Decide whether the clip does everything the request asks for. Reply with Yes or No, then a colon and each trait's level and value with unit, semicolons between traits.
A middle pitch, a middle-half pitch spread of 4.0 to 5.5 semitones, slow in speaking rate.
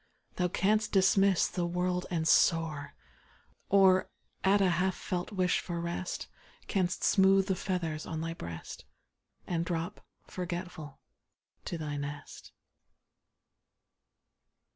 No: medium, 180 Hz; narrow, 2.4 semitones; slow, 115 wpm